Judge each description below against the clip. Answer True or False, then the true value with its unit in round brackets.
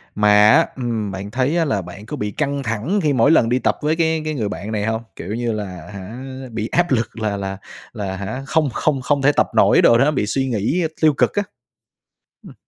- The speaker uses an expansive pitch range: True (5.7 semitones)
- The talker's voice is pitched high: False (120 Hz)